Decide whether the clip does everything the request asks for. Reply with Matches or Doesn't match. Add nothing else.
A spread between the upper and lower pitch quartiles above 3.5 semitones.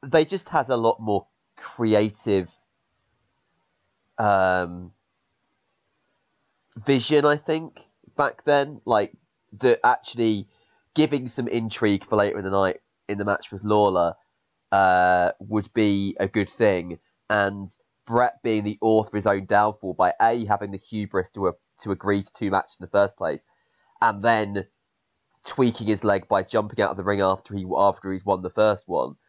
Doesn't match